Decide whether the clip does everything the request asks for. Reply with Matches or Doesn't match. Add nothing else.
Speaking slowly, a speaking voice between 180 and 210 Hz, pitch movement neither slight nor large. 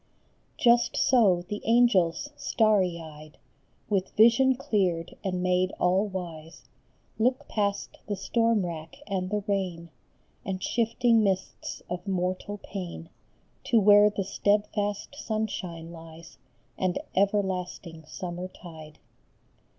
Matches